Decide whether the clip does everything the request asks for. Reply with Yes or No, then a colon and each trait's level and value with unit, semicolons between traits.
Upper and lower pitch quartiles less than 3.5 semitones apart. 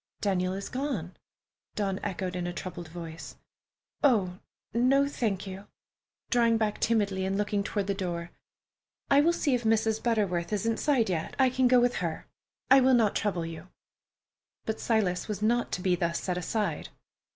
No: average, 4.5 semitones